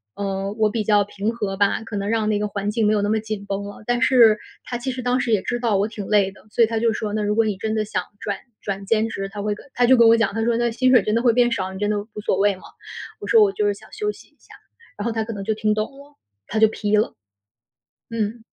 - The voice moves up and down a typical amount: No, narrow, 2.1 semitones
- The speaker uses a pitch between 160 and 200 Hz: No, high, 215 Hz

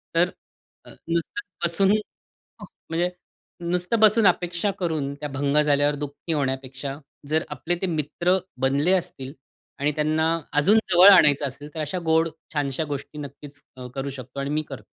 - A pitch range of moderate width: Yes, average, 3.6 semitones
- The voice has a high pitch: No, medium, 150 Hz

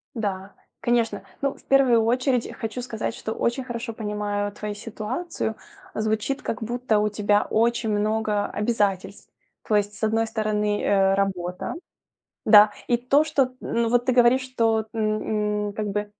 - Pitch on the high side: Yes, high, 220 Hz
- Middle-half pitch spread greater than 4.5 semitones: No, narrow, 2.4 semitones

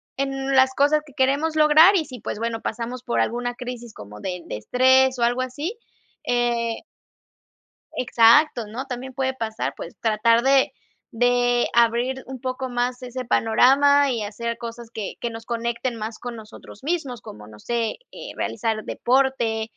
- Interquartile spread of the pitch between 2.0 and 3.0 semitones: Yes, narrow, 2.4 semitones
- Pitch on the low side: No, high, 245 Hz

